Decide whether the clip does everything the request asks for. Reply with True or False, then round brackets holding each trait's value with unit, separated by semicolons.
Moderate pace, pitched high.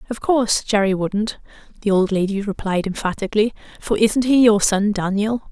True (165 wpm; 215 Hz)